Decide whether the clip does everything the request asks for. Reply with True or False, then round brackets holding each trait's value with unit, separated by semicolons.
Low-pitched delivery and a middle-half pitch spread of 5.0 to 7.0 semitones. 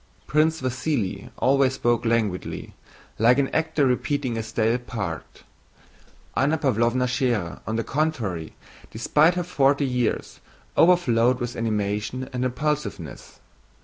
False (125 Hz; 3.9 semitones)